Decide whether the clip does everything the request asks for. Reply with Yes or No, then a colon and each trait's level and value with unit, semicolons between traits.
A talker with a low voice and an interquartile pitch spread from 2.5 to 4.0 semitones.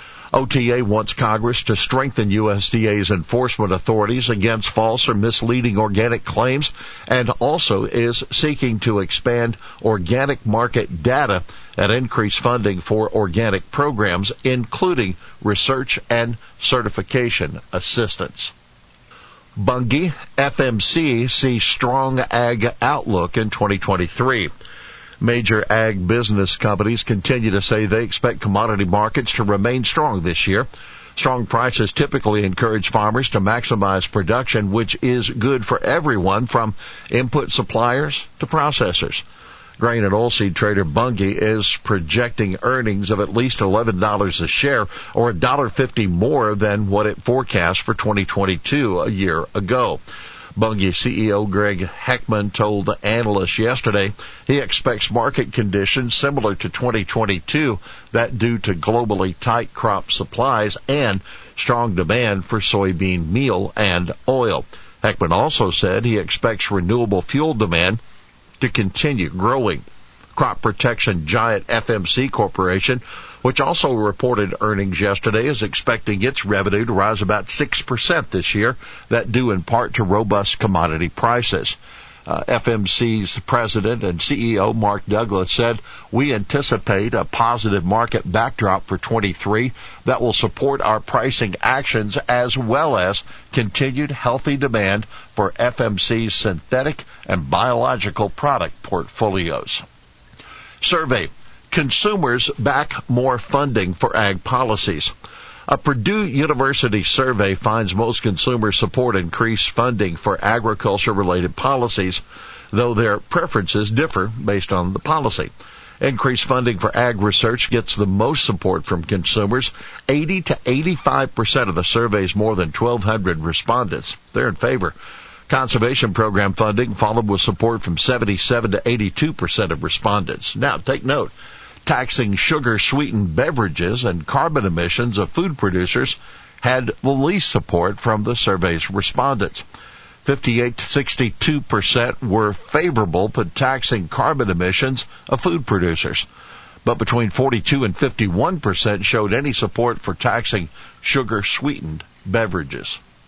Yes: low, 110 Hz; average, 3.6 semitones